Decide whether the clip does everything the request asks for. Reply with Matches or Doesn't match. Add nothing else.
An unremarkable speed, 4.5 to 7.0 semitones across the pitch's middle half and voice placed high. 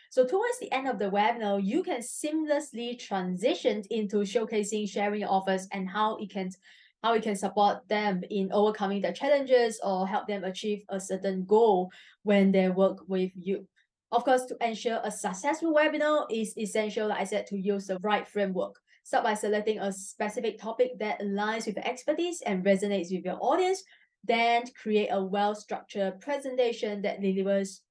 Doesn't match